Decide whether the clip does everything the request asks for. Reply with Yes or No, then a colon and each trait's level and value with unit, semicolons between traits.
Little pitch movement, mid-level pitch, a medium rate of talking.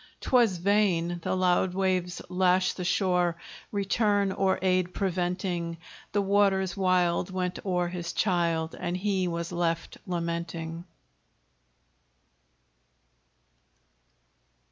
No: narrow, 1.7 semitones; medium, 180 Hz; slow, 100 wpm